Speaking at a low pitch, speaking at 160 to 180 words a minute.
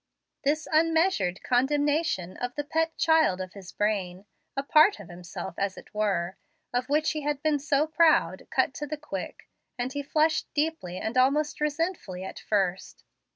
No: very high, 280 Hz; average, 165 wpm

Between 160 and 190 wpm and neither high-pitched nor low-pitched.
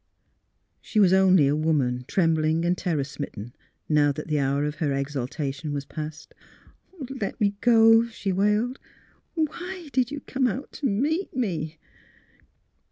Yes: average, 170 wpm; medium, 170 Hz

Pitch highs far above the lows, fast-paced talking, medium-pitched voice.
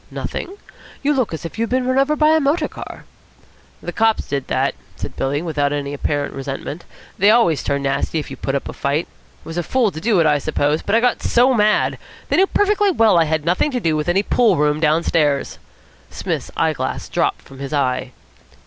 Yes: wide, 8.7 semitones; fast, 225 wpm; medium, 165 Hz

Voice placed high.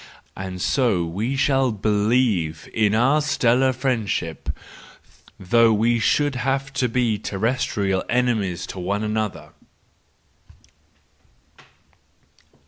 No: low, 115 Hz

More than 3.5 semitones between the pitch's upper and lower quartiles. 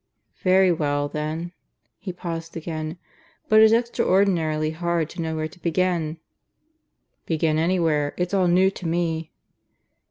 No: narrow, 2.6 semitones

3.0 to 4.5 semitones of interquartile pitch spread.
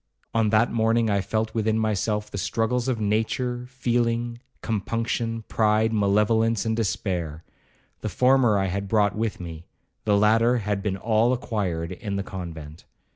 No: narrow, 2.4 semitones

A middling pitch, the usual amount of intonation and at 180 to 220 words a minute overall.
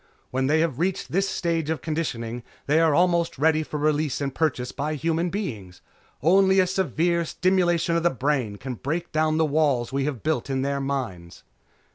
Yes: medium, 155 Hz; average, 3.9 semitones; average, 185 wpm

